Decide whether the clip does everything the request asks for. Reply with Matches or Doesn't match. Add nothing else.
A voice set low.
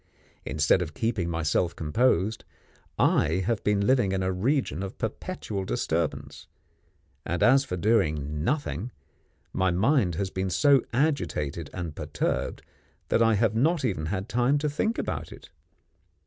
Matches